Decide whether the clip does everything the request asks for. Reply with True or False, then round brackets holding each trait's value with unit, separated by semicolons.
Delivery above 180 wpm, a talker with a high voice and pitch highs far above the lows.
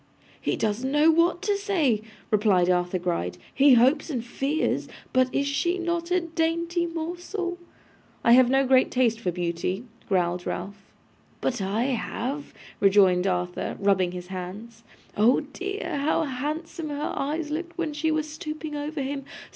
False (155 wpm; 270 Hz; 8.1 semitones)